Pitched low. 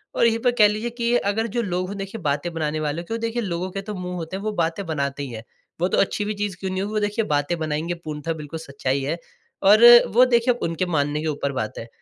No: medium, 180 Hz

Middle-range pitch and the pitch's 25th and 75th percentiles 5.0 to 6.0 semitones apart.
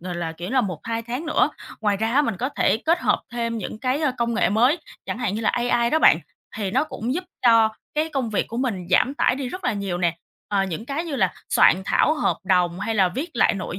No: high, 230 Hz; average, 5.3 semitones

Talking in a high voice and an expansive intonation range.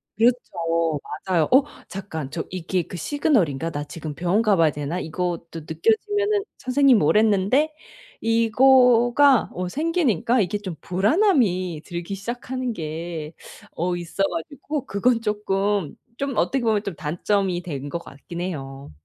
Yes: high, 195 Hz; wide, 6.5 semitones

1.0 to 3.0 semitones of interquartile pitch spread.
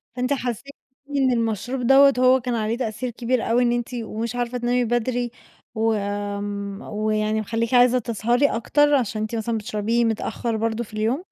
Yes: narrow, 2.4 semitones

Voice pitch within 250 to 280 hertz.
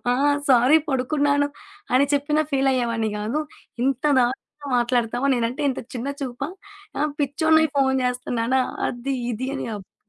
Yes: very high, 265 Hz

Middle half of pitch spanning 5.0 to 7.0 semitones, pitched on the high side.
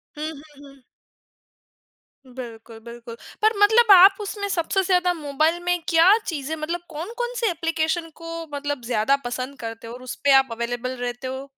Yes: wide, 5.6 semitones; very high, 300 Hz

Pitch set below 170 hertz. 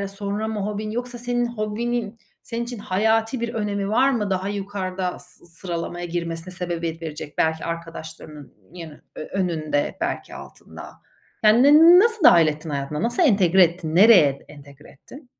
No: high, 190 Hz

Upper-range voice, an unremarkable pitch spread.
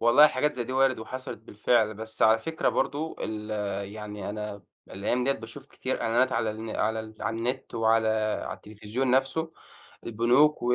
No: low, 115 Hz; average, 3.2 semitones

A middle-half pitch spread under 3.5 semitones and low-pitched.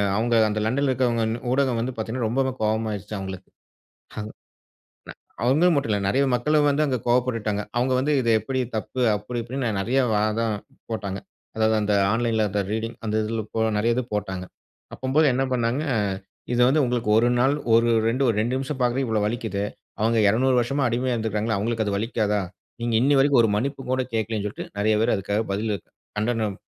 Yes: average, 3.1 semitones; low, 115 Hz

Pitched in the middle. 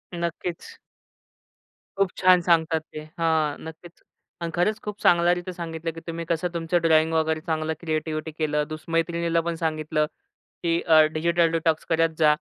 Yes: medium, 165 Hz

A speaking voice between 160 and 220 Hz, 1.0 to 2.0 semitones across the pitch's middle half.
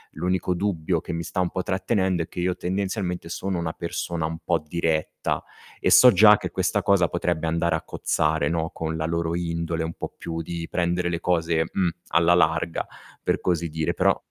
No: very low, 85 Hz; narrow, 1.6 semitones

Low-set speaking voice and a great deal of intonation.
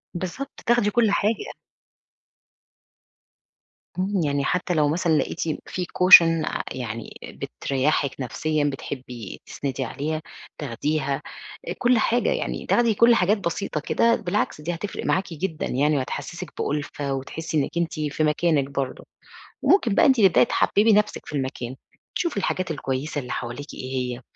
No: medium, 155 Hz; wide, 5.9 semitones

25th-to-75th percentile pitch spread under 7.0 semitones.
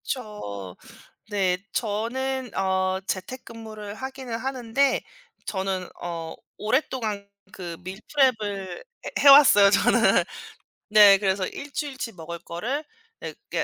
Yes: wide, 5.4 semitones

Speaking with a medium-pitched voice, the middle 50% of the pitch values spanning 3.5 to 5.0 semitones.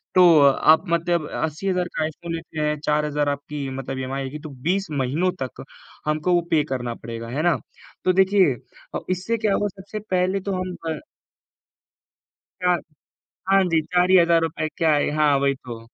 Yes: medium, 160 Hz; average, 4.1 semitones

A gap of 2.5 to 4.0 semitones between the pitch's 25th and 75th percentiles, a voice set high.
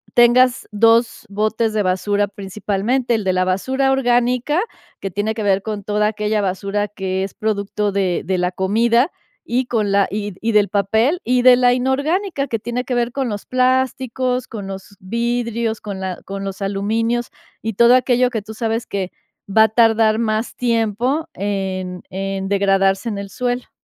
Yes: average, 3.5 semitones; high, 220 Hz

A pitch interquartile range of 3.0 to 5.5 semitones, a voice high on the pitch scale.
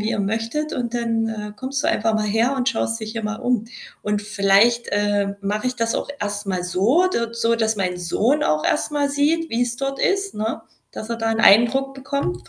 Yes: average, 3.6 semitones; high, 225 Hz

